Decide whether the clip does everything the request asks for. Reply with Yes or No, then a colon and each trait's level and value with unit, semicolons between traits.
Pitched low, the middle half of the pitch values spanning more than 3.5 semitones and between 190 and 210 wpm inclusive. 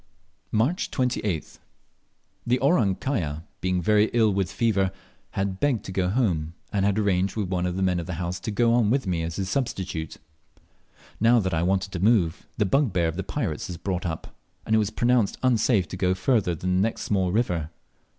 Yes: very low, 95 Hz; average, 4.0 semitones; average, 200 wpm